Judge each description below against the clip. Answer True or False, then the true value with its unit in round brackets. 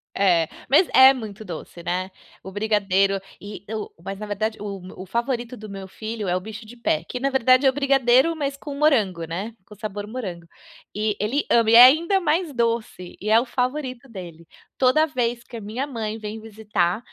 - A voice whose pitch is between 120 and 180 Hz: False (220 Hz)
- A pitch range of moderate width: True (4.3 semitones)